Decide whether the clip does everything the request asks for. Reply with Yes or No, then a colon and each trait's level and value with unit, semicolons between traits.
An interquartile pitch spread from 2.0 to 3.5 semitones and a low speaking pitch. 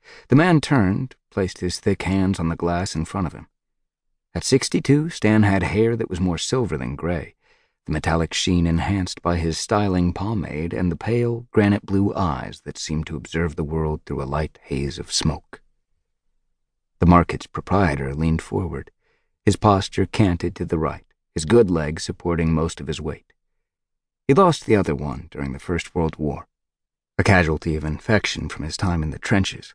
No: average, 4.1 semitones; very low, 85 Hz